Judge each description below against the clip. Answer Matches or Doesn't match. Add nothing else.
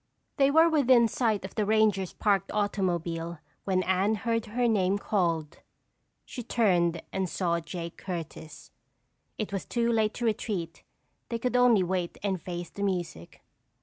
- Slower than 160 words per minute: Matches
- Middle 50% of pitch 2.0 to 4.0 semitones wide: Doesn't match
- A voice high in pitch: Matches